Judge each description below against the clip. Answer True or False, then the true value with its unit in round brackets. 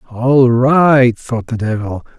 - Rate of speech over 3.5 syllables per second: False (3.2 syllables/s)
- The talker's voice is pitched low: True (125 Hz)